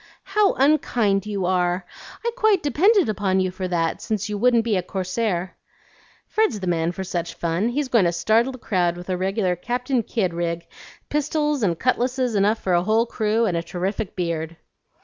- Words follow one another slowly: No, average, 190 wpm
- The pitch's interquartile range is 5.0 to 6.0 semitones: Yes, wide, 5.6 semitones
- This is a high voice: Yes, high, 200 Hz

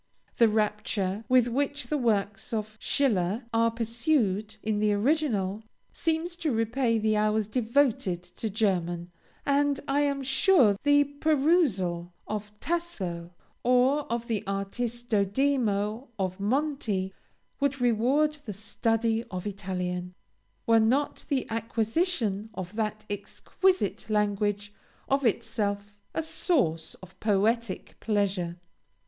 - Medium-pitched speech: No, high, 220 Hz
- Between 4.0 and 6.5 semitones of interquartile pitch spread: Yes, average, 5.1 semitones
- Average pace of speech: No, slow, 115 wpm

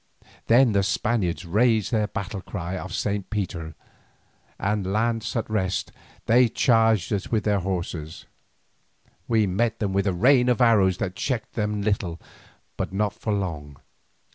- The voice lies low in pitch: Yes, low, 105 Hz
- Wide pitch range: No, average, 3.3 semitones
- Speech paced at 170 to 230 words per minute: No, average, 155 wpm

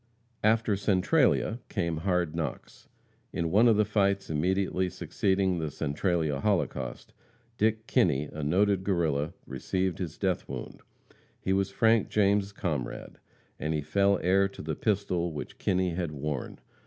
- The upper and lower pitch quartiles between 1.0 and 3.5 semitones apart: No, average, 3.9 semitones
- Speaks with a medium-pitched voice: No, very low, 95 Hz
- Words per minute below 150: Yes, average, 140 wpm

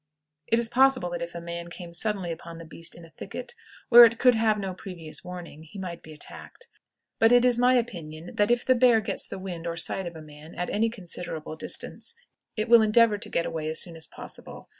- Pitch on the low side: No, medium, 185 Hz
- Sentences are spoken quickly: Yes, fast, 230 wpm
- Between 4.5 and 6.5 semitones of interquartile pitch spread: Yes, wide, 5.4 semitones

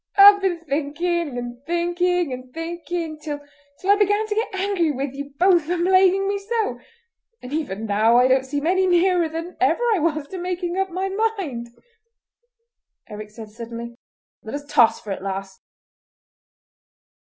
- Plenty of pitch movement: Yes, wide, 6.6 semitones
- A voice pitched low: No, very high, 330 Hz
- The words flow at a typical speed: Yes, average, 160 wpm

